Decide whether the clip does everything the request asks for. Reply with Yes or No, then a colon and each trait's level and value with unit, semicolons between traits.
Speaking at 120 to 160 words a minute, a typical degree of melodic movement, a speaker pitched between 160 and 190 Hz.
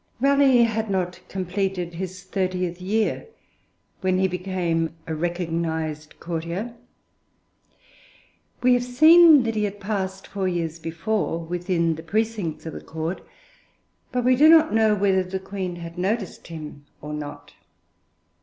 Yes: slow, 135 wpm; average, 4.5 semitones; medium, 185 Hz